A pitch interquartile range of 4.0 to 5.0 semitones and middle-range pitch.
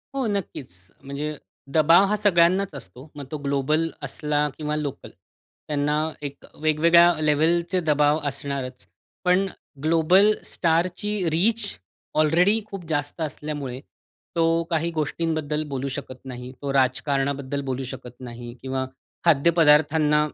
No: average, 3.2 semitones; medium, 150 Hz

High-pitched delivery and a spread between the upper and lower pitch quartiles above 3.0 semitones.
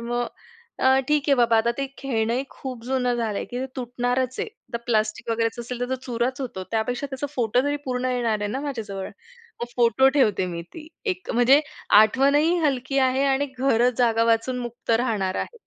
No: high, 245 Hz; average, 2.7 semitones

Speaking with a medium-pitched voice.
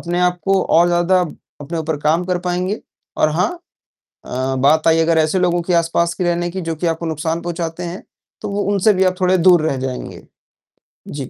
Yes: medium, 175 Hz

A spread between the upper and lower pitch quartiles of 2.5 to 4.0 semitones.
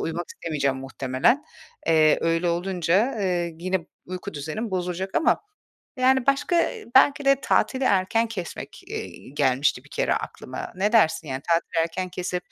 No: wide, 5.4 semitones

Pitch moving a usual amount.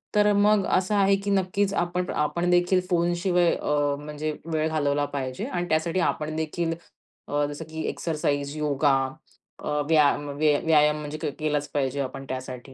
Yes: average, 3.3 semitones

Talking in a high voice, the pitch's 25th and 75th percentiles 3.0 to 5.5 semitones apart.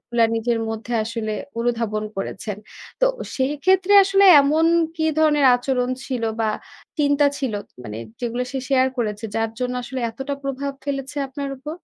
Yes: very high, 260 Hz; average, 3.8 semitones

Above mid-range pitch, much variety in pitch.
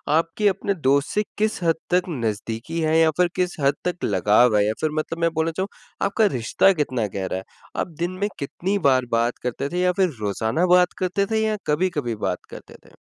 No: medium, 160 Hz; wide, 6.9 semitones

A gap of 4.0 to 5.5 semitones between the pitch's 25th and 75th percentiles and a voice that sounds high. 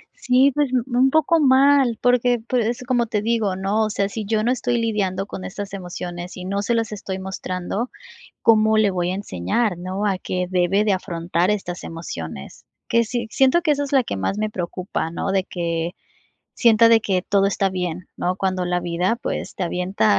Yes: average, 4.4 semitones; high, 200 Hz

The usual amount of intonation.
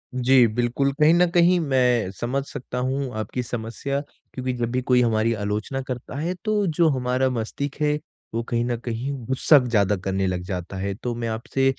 Yes: average, 3.2 semitones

